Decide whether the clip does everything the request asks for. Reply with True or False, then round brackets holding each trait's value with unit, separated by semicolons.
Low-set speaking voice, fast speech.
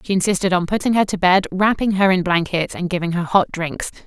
False (185 Hz; 235 wpm)